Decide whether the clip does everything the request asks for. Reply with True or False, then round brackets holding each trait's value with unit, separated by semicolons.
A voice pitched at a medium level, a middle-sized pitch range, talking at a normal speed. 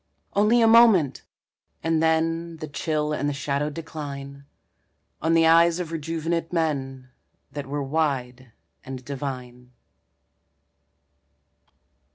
False (150 Hz; 3.0 semitones; 110 wpm)